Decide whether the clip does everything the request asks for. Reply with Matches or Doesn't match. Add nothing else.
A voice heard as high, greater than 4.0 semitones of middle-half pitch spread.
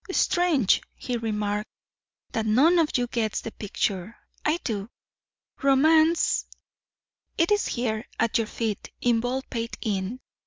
Matches